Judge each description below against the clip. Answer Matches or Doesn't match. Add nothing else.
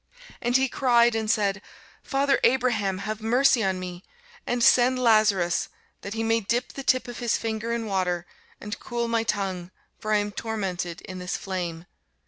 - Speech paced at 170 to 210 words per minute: Matches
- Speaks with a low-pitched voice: Doesn't match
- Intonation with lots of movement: Doesn't match